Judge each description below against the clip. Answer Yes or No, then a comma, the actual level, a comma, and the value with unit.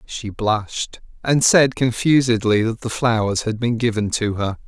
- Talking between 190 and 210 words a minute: No, average, 165 wpm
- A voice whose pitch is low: Yes, low, 115 Hz